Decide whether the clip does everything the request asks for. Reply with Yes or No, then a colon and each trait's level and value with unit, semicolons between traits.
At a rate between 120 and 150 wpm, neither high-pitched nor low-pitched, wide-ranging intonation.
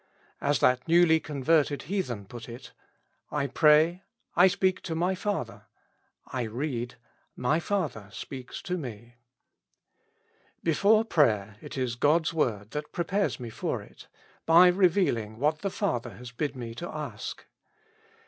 Yes: average, 140 wpm; medium, 150 Hz; wide, 6.3 semitones